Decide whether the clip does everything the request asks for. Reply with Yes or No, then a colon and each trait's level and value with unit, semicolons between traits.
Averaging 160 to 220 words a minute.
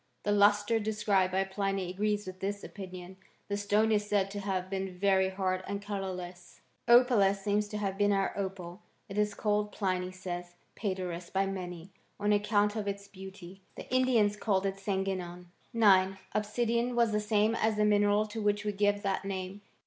Yes: average, 180 wpm